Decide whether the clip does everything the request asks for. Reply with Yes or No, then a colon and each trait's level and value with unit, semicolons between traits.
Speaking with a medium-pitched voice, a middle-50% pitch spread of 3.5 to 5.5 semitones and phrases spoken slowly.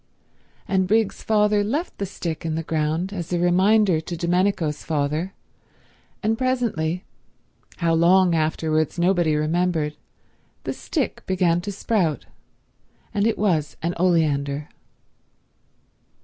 Yes: medium, 175 Hz; average, 3.8 semitones; slow, 110 wpm